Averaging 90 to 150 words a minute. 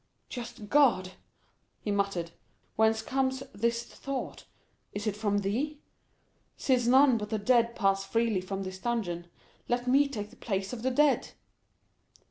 Yes: average, 145 wpm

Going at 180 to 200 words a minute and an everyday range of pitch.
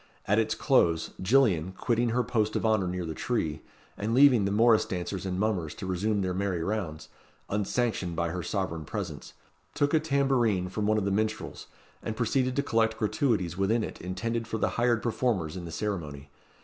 Yes: average, 190 wpm; average, 4.2 semitones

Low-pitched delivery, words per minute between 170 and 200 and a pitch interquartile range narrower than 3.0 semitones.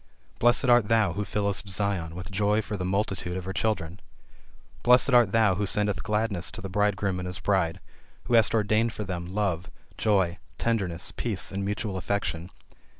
Yes: low, 100 Hz; average, 175 wpm; narrow, 2.6 semitones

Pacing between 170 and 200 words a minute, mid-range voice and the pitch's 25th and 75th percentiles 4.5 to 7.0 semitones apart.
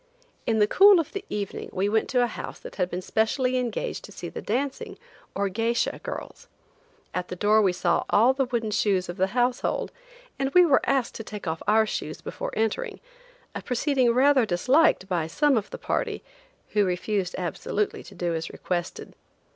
No: average, 190 wpm; high, 220 Hz; average, 5.2 semitones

